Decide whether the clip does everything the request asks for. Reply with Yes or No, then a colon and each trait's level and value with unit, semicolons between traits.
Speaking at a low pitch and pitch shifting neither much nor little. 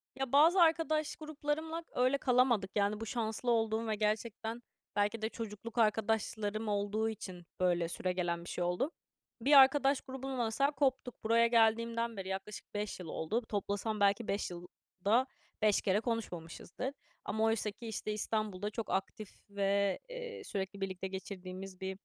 No: high, 220 Hz; average, 3.7 semitones